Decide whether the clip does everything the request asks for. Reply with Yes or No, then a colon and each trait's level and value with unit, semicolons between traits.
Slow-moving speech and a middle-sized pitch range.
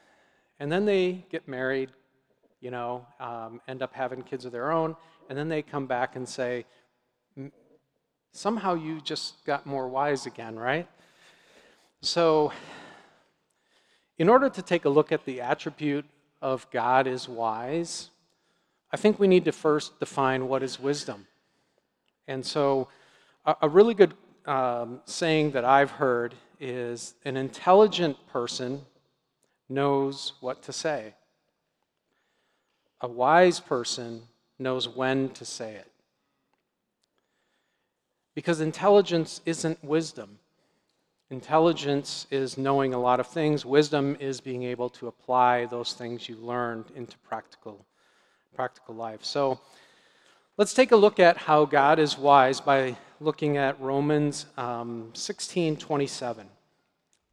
Yes: slow, 130 wpm; average, 3.9 semitones